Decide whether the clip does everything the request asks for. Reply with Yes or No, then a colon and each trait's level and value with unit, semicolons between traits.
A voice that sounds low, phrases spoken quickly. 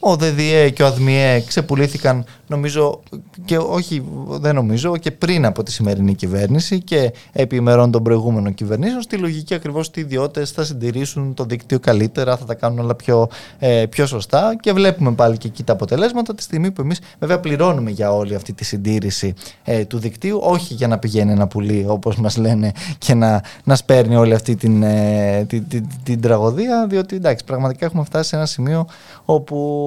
Yes: low, 130 Hz; fast, 185 wpm